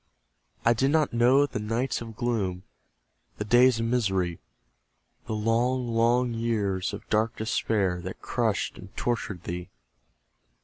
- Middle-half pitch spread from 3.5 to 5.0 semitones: No, average, 3.0 semitones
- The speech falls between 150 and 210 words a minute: No, slow, 135 wpm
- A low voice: Yes, low, 115 Hz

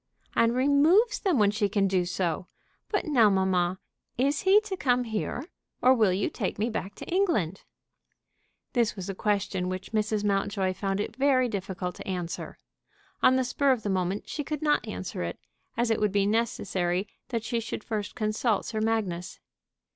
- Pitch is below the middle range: No, high, 215 Hz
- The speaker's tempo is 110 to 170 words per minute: No, average, 180 wpm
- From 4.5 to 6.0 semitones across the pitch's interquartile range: Yes, average, 4.8 semitones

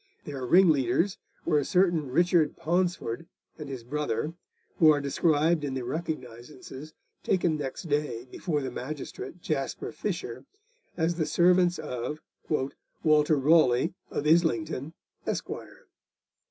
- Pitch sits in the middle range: Yes, medium, 150 Hz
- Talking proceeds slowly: Yes, slow, 120 wpm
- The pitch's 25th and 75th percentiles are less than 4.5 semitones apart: Yes, average, 3.9 semitones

